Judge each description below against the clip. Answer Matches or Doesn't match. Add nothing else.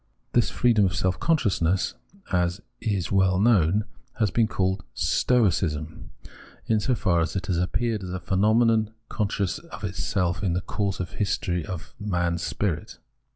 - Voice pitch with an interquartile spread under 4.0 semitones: Matches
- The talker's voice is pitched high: Doesn't match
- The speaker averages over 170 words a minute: Doesn't match